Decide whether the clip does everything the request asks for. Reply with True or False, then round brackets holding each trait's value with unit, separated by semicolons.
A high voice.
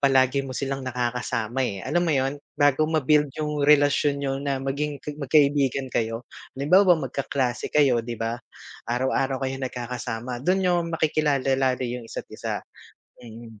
False (135 Hz)